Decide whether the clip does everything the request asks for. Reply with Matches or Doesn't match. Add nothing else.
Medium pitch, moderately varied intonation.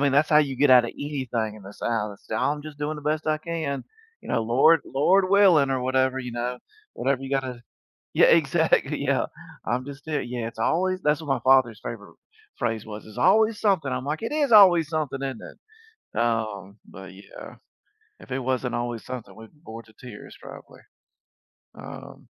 Doesn't match